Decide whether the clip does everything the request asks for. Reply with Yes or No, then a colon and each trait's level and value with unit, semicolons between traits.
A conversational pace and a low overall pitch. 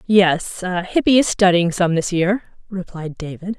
No: average, 150 wpm; medium, 185 Hz